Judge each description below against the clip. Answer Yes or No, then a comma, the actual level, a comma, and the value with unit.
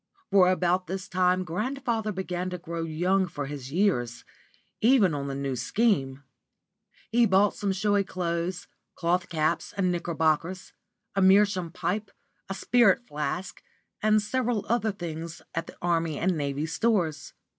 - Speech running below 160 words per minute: Yes, average, 145 wpm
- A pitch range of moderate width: Yes, average, 3.7 semitones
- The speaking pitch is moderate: Yes, medium, 180 Hz